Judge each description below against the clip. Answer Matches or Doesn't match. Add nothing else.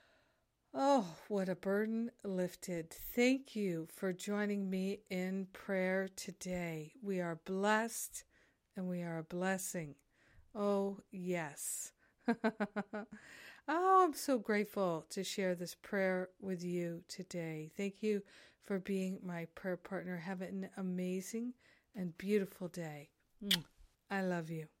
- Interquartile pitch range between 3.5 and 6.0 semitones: Doesn't match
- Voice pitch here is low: Doesn't match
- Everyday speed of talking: Doesn't match